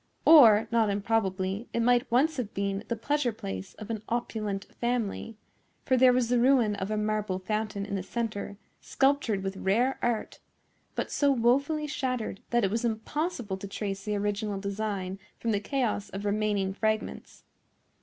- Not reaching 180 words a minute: Yes, average, 165 wpm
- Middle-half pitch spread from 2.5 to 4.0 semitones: Yes, average, 3.4 semitones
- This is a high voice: Yes, high, 215 Hz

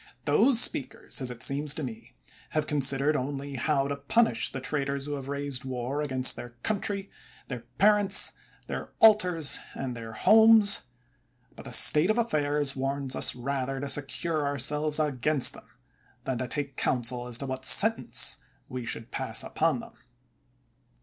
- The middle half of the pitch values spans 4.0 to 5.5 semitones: No, average, 2.9 semitones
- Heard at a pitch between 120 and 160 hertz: Yes, medium, 140 Hz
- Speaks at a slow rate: No, average, 165 wpm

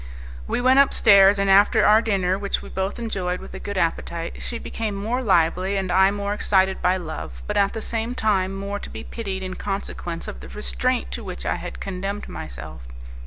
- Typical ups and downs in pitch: No, narrow, 2.3 semitones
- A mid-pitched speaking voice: No, high, 195 Hz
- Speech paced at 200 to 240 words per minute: Yes, fast, 205 wpm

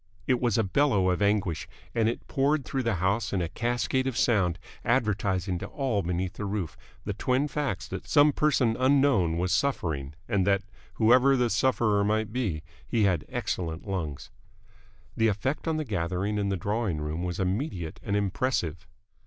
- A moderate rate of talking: Yes, average, 175 wpm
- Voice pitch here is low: Yes, low, 105 Hz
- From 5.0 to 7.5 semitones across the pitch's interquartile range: Yes, wide, 5.6 semitones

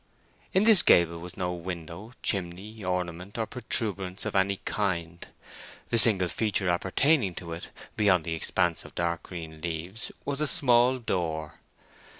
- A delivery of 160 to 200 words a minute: No, average, 150 wpm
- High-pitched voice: No, very low, 95 Hz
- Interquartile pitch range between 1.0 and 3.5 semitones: No, average, 4.4 semitones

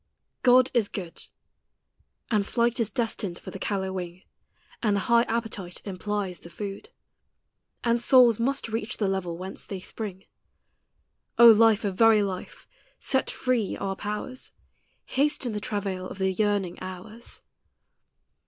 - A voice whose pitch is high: Yes, high, 210 Hz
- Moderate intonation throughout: Yes, average, 3.5 semitones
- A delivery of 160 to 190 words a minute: No, average, 150 wpm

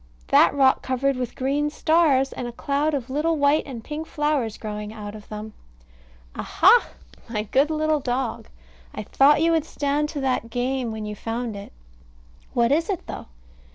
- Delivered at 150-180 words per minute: Yes, average, 175 wpm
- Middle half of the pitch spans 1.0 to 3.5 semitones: No, average, 4.4 semitones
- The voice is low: No, very high, 265 Hz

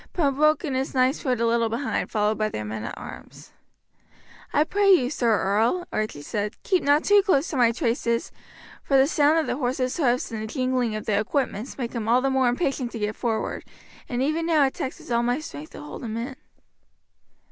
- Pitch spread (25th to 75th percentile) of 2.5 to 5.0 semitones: Yes, average, 4.1 semitones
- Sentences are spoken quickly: Yes, fast, 210 wpm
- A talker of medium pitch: No, very high, 250 Hz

